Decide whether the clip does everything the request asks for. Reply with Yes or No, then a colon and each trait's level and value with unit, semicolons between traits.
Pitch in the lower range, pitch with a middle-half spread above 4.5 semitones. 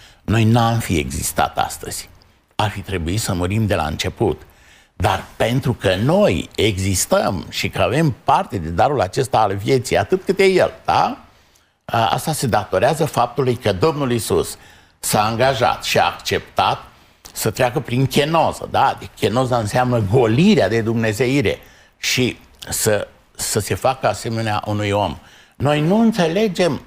Yes: low, 115 Hz; average, 5.0 semitones